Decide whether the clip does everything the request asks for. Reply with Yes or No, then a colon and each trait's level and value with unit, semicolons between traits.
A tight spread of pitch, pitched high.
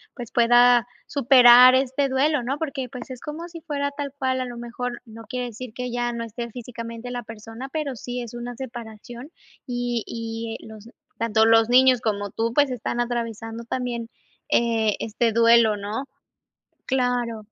Yes: narrow, 1.9 semitones; high, 240 Hz